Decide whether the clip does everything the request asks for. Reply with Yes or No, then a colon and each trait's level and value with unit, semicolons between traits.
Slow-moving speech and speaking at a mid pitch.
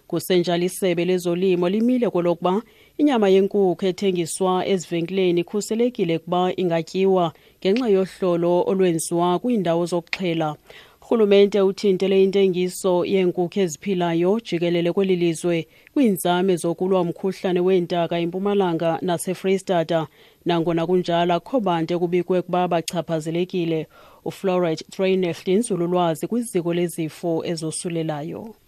Yes: slow, 90 wpm; medium, 180 Hz